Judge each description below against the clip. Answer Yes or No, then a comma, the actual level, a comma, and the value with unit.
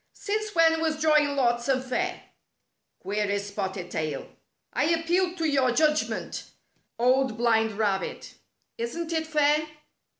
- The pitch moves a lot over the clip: Yes, wide, 6.4 semitones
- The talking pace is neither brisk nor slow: No, slow, 130 wpm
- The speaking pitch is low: No, very high, 280 Hz